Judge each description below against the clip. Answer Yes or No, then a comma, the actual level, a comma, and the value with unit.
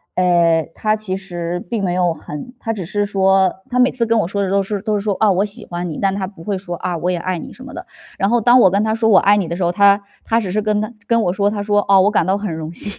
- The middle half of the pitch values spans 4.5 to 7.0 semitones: No, average, 2.8 semitones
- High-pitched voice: Yes, high, 195 Hz